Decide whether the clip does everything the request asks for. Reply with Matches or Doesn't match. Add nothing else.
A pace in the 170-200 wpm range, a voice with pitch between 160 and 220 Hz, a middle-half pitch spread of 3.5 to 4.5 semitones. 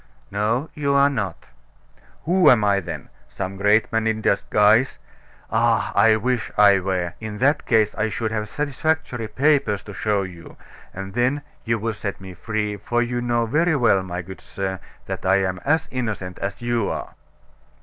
Doesn't match